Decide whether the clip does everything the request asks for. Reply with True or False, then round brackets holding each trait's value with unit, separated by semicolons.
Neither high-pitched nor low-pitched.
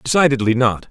False (130 Hz)